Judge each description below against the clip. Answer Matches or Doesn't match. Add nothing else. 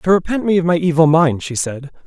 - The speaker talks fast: Matches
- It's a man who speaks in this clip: Matches